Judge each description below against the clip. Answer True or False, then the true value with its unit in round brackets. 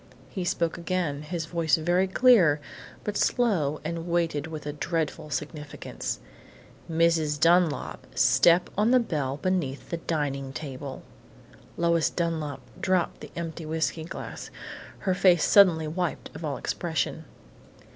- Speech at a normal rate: False (130 wpm)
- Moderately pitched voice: True (165 Hz)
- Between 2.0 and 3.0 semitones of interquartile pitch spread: True (2.7 semitones)